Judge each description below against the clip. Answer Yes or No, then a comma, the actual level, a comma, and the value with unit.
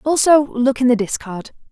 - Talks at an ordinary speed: Yes, average, 175 wpm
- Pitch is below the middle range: No, very high, 255 Hz